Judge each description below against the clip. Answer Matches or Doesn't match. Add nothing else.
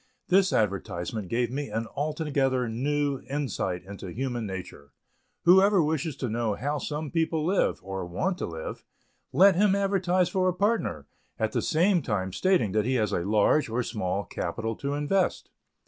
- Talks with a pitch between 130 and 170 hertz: Matches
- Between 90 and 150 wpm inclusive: Doesn't match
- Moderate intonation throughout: Doesn't match